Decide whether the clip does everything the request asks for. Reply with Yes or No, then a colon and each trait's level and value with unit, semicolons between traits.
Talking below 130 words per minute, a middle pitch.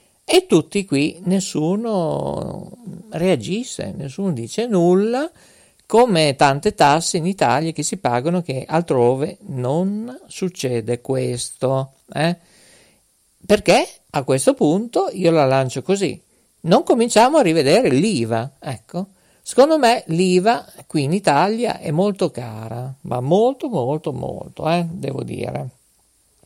Yes: average, 120 wpm; medium, 170 Hz